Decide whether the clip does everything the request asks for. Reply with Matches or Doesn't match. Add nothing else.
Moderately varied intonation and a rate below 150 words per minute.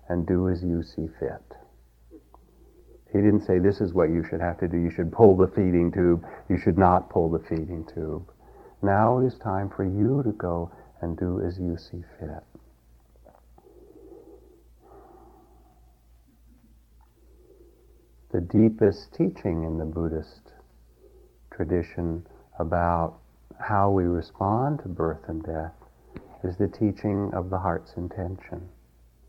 Matches